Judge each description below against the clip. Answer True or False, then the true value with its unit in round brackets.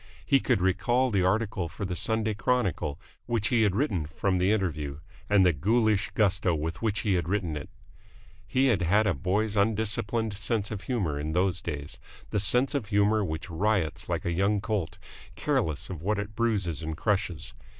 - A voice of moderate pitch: False (100 Hz)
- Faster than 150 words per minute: True (185 wpm)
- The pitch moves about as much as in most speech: True (4.0 semitones)